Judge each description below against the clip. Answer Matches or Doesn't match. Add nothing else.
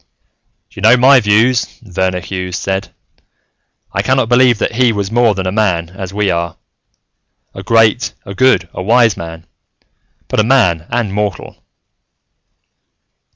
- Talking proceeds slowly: Doesn't match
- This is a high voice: Doesn't match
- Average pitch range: Matches